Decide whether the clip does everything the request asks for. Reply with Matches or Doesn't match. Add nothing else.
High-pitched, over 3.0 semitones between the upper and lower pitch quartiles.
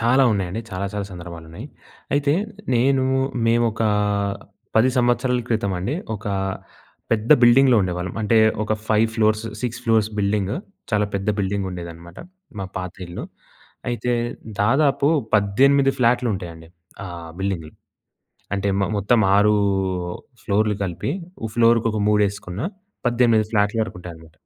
Doesn't match